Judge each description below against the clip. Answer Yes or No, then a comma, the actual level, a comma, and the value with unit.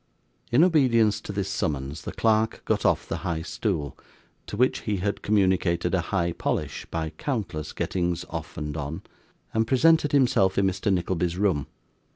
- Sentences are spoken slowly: No, average, 165 wpm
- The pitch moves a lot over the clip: No, average, 4.8 semitones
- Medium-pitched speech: No, very low, 95 Hz